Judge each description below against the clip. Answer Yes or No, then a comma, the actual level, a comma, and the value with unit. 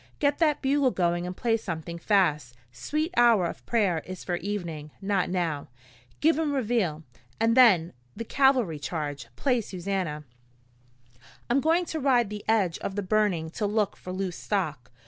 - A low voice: No, high, 195 Hz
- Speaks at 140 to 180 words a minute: Yes, average, 165 wpm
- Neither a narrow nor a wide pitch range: No, wide, 6.0 semitones